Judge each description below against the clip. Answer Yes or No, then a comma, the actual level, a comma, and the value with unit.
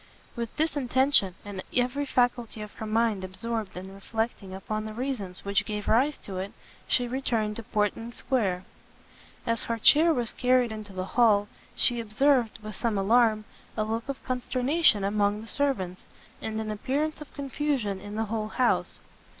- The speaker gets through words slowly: No, average, 165 wpm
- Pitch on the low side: No, high, 225 Hz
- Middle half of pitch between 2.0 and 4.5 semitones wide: Yes, average, 3.6 semitones